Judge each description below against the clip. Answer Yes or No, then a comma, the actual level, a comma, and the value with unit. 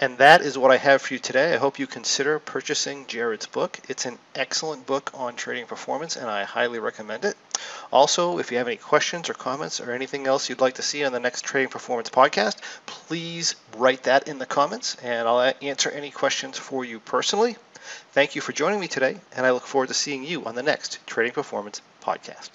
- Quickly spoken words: Yes, fast, 220 wpm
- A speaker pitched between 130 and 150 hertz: Yes, low, 135 Hz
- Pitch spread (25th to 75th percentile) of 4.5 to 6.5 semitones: No, average, 3.3 semitones